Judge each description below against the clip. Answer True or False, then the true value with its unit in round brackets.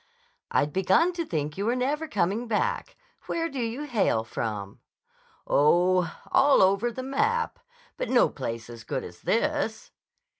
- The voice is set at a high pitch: True (225 Hz)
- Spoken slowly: False (150 wpm)